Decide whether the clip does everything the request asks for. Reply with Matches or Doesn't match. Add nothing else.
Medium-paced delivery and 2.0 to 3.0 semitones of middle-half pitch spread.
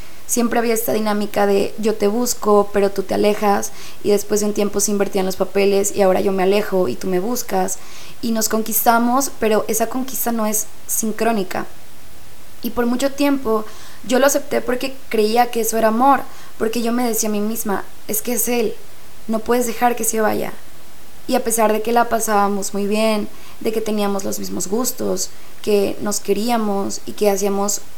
Doesn't match